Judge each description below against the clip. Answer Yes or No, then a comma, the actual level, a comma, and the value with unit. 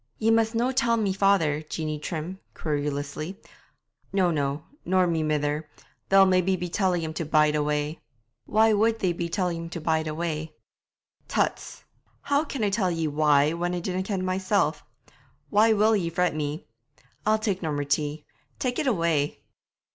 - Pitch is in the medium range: Yes, medium, 170 Hz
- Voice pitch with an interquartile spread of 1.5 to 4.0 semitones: No, average, 4.5 semitones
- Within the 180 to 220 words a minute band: No, average, 170 wpm